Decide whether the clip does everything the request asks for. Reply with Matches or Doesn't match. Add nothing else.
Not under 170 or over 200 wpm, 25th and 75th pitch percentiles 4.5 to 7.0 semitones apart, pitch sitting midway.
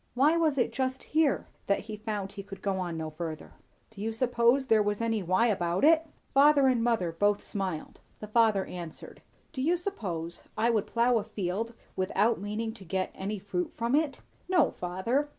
Doesn't match